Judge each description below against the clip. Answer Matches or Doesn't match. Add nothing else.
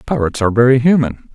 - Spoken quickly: Doesn't match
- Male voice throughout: Matches